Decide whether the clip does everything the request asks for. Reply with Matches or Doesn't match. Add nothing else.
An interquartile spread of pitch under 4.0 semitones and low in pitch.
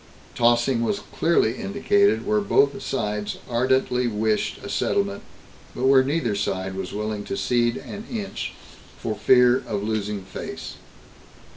Doesn't match